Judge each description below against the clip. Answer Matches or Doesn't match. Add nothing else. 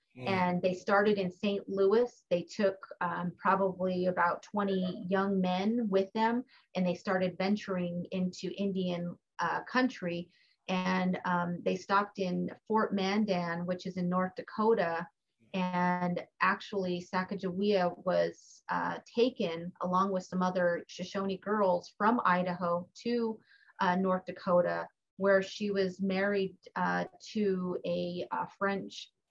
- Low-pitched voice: Doesn't match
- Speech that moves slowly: Matches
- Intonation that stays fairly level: Matches